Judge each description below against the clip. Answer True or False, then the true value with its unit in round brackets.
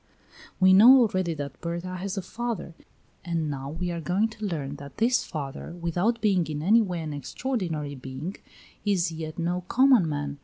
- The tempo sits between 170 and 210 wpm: True (180 wpm)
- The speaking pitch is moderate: True (175 Hz)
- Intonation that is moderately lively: True (4.7 semitones)